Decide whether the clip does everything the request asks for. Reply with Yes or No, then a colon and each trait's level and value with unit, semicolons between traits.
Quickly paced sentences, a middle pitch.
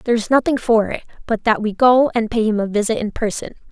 No: fast, 260 wpm; high, 225 Hz